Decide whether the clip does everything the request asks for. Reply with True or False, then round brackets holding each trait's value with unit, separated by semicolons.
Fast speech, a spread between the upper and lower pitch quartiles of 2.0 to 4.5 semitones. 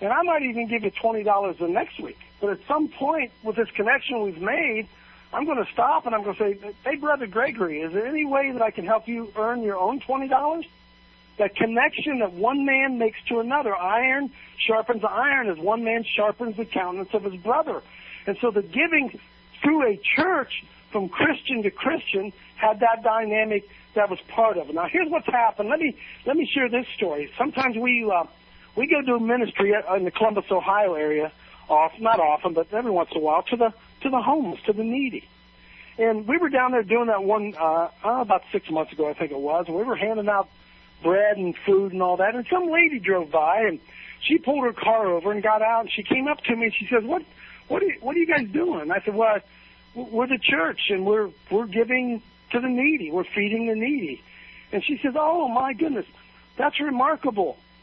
False (220 wpm; 4.9 semitones)